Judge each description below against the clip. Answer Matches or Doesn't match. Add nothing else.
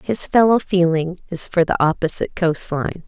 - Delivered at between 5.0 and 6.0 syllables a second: Doesn't match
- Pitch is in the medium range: Matches